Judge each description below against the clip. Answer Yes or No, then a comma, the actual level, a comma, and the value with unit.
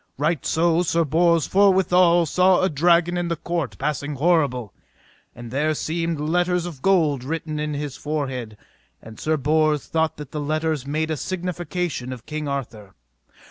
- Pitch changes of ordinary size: Yes, average, 3.2 semitones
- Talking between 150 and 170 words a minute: Yes, average, 160 wpm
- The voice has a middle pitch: Yes, medium, 155 Hz